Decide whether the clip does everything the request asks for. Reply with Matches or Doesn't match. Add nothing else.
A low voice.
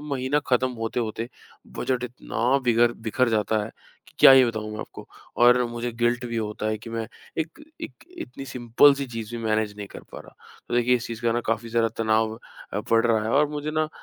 Matches